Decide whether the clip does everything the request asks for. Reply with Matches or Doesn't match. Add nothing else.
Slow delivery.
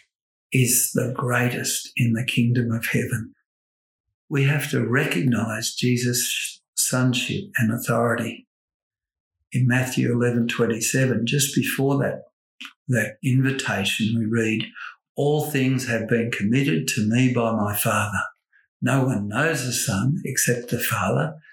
Matches